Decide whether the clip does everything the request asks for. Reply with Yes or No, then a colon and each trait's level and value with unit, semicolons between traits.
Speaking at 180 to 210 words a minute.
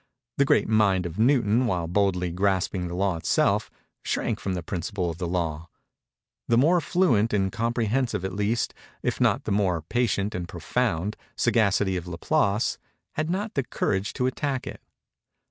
No: average, 165 wpm